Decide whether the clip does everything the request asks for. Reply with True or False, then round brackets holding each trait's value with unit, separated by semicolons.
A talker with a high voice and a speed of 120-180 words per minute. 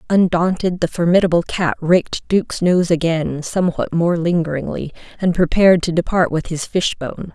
False (170 Hz; 145 wpm)